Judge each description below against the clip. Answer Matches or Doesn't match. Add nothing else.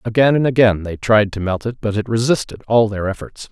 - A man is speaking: Matches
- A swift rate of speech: Matches